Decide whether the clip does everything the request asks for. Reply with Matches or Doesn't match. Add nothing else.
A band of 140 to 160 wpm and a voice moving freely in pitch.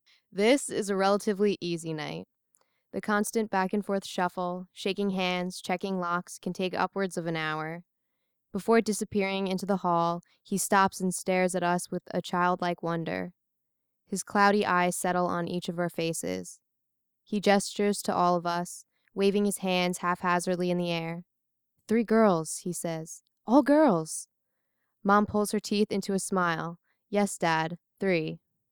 Doesn't match